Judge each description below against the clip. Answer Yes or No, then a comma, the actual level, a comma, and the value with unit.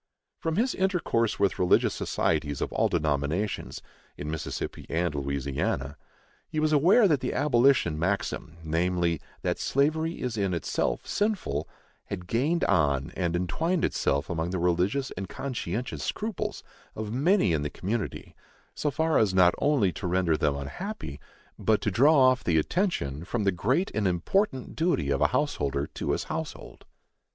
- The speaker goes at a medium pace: Yes, average, 155 wpm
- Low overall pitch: Yes, very low, 95 Hz